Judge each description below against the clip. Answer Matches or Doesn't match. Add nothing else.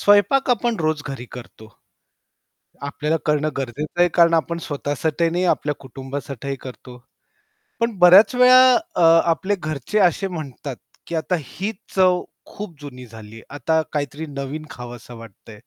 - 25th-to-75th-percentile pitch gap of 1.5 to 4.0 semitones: Doesn't match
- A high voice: Doesn't match